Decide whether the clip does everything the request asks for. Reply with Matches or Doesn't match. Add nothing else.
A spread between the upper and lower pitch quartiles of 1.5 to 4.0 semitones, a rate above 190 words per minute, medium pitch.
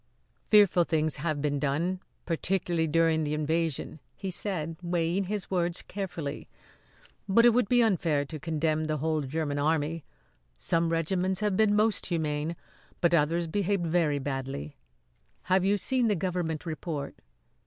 Doesn't match